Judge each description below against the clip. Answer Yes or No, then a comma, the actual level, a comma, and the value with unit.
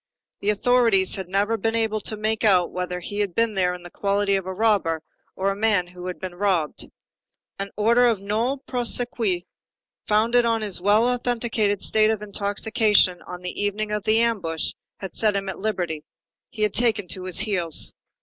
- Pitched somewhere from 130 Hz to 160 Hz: No, high, 205 Hz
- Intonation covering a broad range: No, average, 3.1 semitones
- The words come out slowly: No, average, 190 wpm